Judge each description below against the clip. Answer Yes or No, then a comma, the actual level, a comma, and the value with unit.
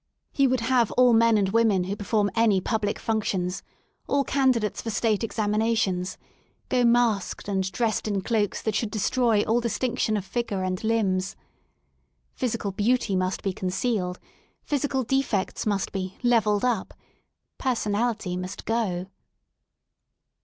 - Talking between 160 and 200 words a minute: No, average, 140 wpm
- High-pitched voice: Yes, high, 215 Hz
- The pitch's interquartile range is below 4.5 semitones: Yes, average, 3.4 semitones